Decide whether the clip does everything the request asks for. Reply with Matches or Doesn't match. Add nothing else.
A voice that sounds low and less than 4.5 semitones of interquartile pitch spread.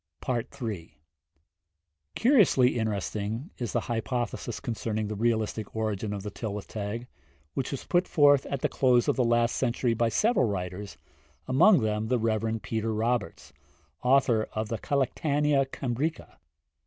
Matches